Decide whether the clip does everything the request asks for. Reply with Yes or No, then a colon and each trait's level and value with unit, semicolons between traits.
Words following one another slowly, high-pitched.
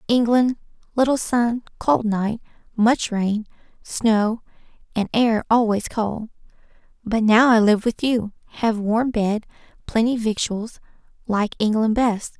Yes: slow, 125 wpm; high, 225 Hz